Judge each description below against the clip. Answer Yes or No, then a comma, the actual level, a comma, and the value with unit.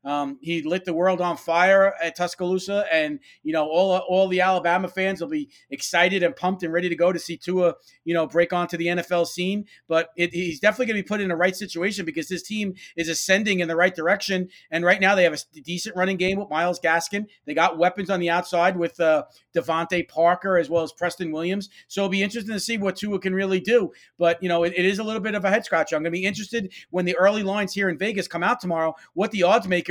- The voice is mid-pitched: Yes, medium, 180 Hz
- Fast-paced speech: Yes, fast, 255 wpm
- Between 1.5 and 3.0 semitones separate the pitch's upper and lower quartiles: Yes, narrow, 2.4 semitones